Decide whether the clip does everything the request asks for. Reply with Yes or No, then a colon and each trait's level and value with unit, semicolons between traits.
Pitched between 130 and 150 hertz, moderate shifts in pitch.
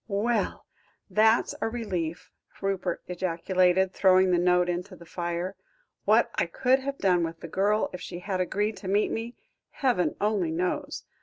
No: medium, 185 Hz; average, 3.2 semitones